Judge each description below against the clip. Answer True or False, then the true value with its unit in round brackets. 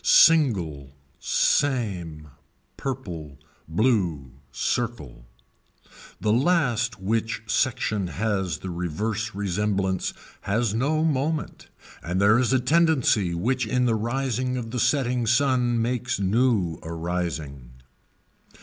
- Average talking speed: False (105 wpm)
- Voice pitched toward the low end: True (110 Hz)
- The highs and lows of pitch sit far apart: True (6.1 semitones)